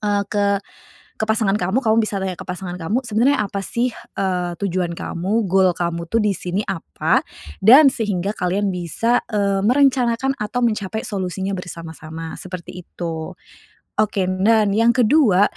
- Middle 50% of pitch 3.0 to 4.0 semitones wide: Yes, average, 3.5 semitones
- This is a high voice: Yes, high, 200 Hz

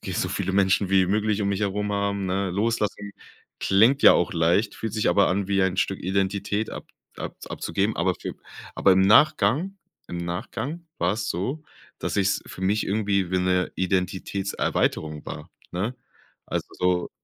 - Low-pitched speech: Yes, low, 100 Hz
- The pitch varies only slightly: Yes, narrow, 2.2 semitones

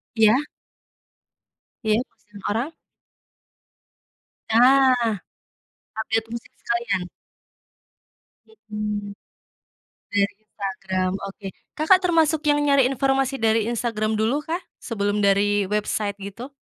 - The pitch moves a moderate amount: Yes, average, 3.9 semitones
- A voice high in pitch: Yes, high, 220 Hz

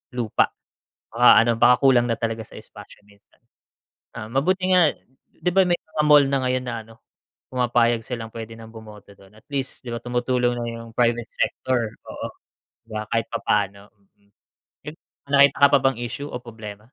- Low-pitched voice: Yes, low, 120 Hz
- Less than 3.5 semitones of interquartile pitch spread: Yes, average, 3.1 semitones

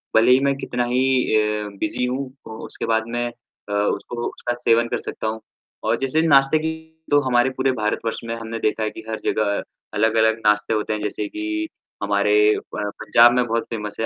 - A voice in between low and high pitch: No, low, 115 Hz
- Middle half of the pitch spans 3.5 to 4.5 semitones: No, average, 2.8 semitones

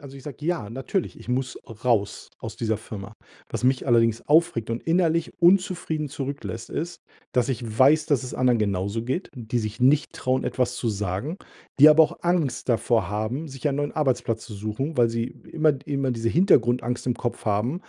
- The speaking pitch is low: Yes, low, 125 Hz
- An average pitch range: Yes, average, 4.7 semitones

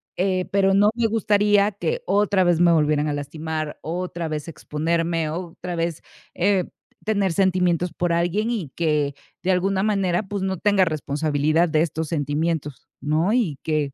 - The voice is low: No, medium, 175 Hz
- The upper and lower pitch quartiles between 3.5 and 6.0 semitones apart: Yes, average, 3.9 semitones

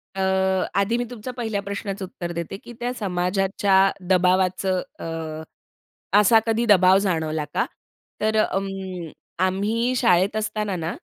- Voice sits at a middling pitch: No, high, 195 Hz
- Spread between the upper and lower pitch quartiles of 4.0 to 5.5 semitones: No, average, 2.8 semitones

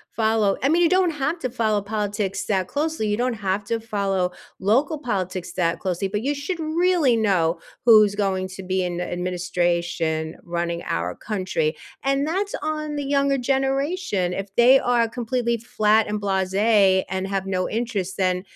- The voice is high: Yes, high, 210 Hz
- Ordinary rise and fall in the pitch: No, wide, 6.1 semitones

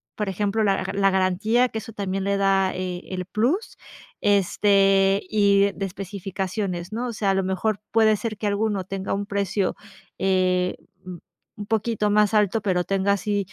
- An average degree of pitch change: No, narrow, 1.8 semitones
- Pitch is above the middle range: Yes, high, 200 Hz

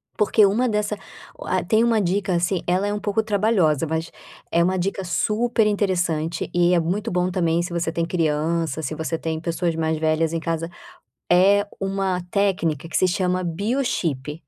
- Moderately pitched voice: Yes, medium, 180 Hz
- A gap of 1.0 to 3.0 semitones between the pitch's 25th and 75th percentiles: No, average, 3.5 semitones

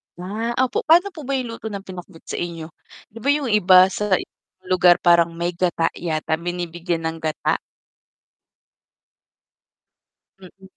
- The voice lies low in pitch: No, medium, 180 Hz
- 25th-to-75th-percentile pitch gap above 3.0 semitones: Yes, average, 3.7 semitones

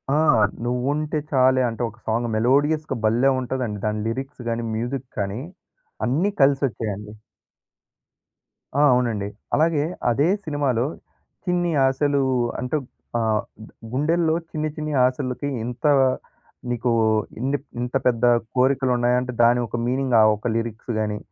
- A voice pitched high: No, low, 125 Hz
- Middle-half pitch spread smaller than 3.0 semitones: No, average, 3.5 semitones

